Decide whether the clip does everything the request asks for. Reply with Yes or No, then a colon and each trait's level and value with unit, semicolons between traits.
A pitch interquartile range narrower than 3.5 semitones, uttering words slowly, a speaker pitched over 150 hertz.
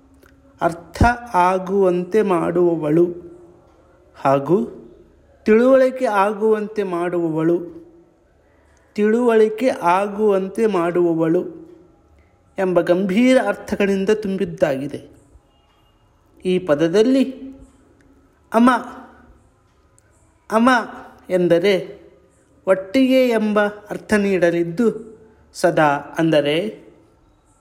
No: average, 4.4 semitones; slow, 55 wpm; high, 190 Hz